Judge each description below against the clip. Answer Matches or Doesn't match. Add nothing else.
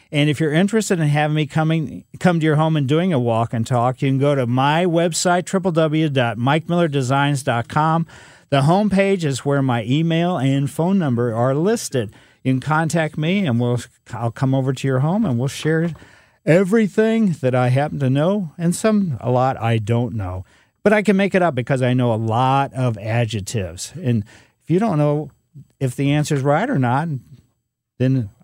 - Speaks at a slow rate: Doesn't match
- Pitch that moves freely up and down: Doesn't match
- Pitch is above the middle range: Doesn't match